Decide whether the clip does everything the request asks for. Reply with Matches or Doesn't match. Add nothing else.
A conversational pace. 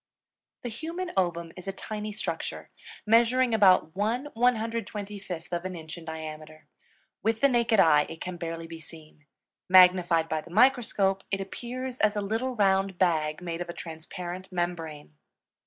Matches